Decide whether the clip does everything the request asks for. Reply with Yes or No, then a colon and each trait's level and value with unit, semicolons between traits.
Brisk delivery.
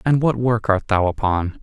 Yes: fast, 220 wpm